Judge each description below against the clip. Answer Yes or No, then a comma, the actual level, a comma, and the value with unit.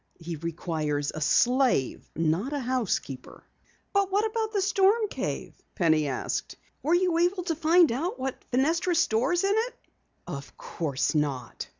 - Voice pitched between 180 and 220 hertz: No, very high, 265 Hz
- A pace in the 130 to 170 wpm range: Yes, average, 150 wpm